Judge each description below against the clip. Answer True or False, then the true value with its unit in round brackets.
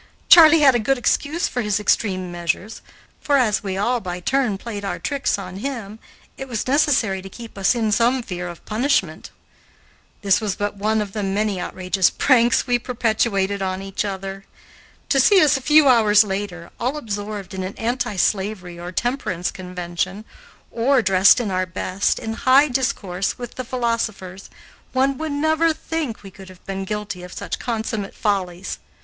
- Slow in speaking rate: False (175 wpm)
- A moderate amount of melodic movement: True (4.6 semitones)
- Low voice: False (210 Hz)